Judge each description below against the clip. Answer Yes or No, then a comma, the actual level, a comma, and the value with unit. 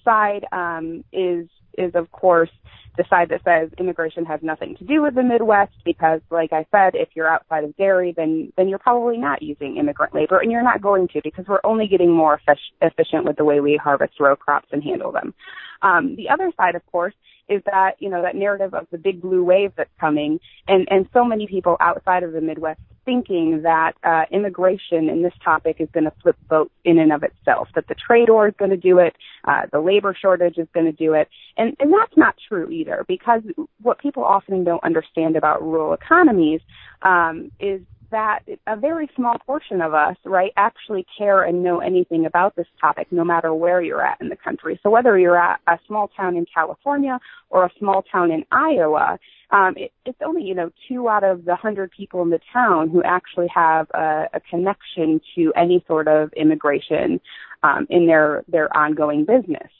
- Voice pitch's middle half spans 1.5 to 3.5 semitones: No, average, 4.1 semitones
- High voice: No, medium, 180 Hz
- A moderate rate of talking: No, fast, 210 wpm